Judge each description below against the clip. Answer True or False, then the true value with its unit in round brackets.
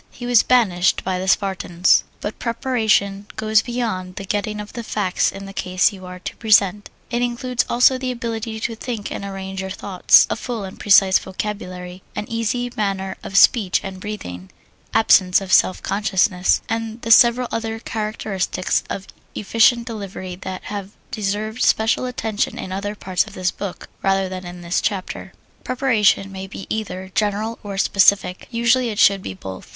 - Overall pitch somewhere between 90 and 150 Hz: False (205 Hz)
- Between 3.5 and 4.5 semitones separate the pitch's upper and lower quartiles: False (3.1 semitones)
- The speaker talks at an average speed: True (170 wpm)